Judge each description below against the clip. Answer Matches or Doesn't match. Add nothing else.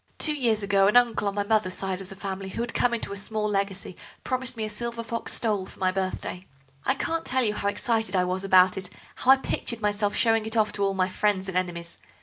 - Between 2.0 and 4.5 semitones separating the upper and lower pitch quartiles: Matches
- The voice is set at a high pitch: Matches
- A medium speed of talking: Doesn't match